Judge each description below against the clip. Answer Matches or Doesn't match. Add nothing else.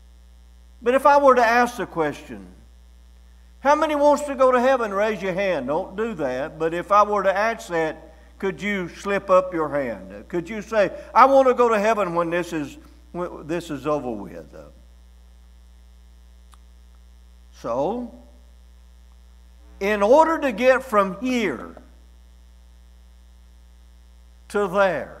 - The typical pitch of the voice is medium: Matches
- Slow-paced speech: Doesn't match